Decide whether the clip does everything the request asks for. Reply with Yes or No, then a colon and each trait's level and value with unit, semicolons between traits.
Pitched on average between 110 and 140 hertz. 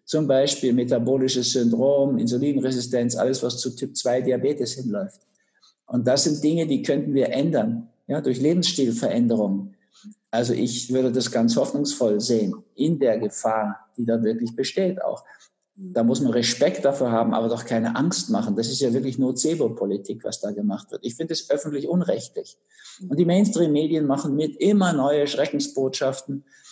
Yes: low, 135 Hz